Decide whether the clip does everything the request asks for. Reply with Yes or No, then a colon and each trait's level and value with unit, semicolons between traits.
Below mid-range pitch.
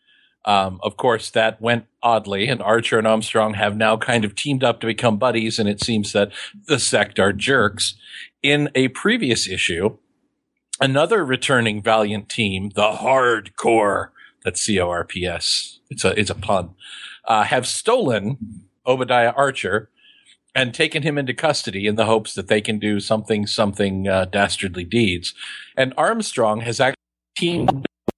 Yes: low, 110 Hz